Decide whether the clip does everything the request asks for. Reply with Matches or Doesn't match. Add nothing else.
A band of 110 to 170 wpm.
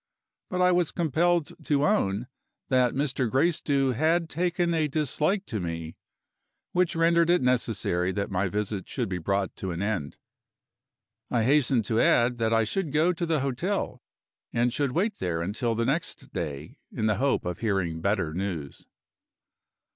Matches